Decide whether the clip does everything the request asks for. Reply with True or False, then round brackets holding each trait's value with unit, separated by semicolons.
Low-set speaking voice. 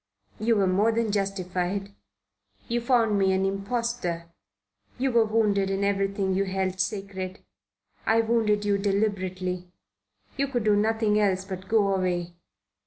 False (200 Hz)